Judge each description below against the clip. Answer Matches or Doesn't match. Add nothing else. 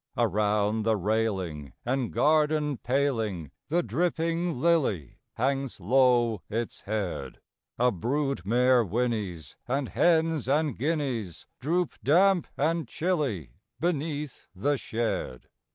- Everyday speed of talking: Doesn't match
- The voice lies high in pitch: Doesn't match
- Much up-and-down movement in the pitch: Matches